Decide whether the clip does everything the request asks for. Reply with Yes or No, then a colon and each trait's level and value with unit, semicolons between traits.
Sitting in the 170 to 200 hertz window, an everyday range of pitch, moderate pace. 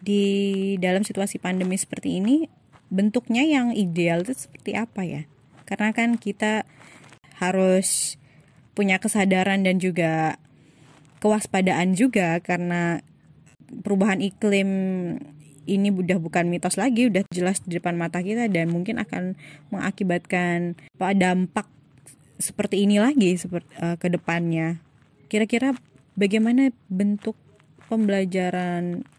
Yes: medium, 185 Hz; average, 3.3 semitones; average, 105 wpm